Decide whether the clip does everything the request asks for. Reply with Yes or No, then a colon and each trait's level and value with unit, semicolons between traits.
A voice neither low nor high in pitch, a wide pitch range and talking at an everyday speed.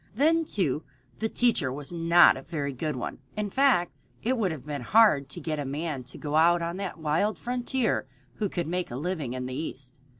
No: medium, 165 Hz; wide, 6.3 semitones; fast, 210 wpm